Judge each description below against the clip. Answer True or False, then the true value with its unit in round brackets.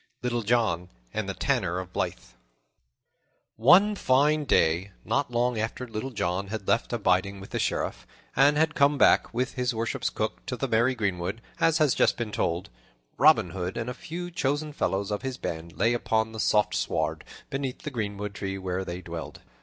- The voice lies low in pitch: True (115 Hz)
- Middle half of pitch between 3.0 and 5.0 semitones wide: False (5.5 semitones)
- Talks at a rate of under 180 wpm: False (185 wpm)